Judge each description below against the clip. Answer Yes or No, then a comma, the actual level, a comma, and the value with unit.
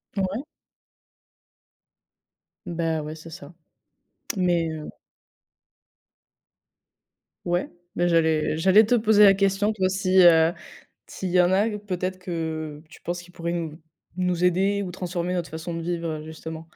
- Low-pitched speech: No, medium, 175 Hz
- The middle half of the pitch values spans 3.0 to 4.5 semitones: No, narrow, 2.5 semitones